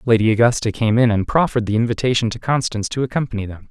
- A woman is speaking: No, male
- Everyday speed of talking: No, fast, 210 wpm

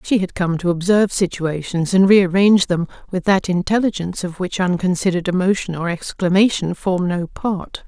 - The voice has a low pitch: No, medium, 185 Hz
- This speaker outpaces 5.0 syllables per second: Yes, 5.3 syllables/s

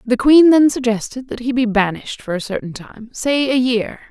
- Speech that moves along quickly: Yes, fast, 220 wpm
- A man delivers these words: No, female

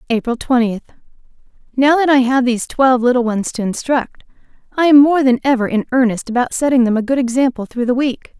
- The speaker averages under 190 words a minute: No, average, 195 wpm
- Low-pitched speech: No, very high, 250 Hz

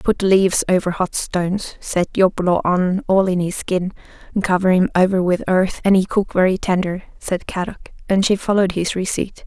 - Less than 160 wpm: No, average, 185 wpm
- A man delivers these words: No, female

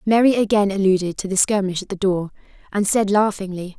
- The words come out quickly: No, average, 190 wpm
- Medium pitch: No, high, 200 Hz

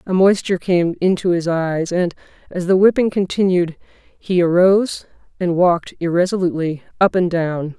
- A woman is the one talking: Yes, female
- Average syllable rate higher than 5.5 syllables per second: No, 5.1 syllables/s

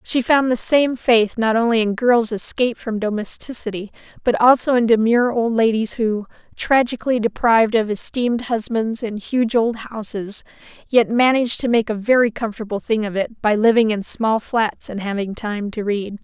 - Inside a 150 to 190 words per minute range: Yes, average, 175 wpm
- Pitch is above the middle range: Yes, high, 225 Hz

